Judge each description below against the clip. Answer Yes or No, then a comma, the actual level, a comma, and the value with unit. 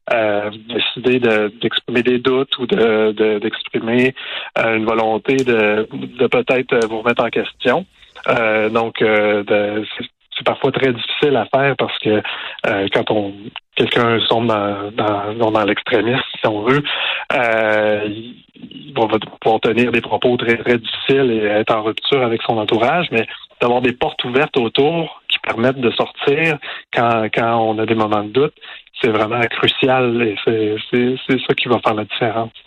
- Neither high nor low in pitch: No, low, 115 Hz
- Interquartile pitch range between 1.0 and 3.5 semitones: Yes, narrow, 2.5 semitones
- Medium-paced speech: Yes, average, 165 wpm